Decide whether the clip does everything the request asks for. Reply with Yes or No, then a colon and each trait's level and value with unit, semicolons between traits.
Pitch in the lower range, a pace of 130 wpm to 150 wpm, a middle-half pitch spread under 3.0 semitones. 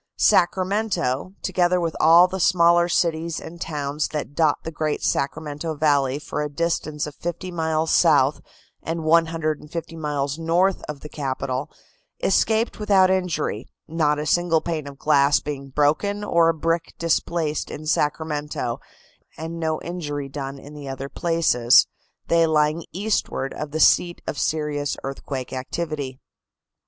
No: medium, 155 Hz; average, 140 wpm; narrow, 2.6 semitones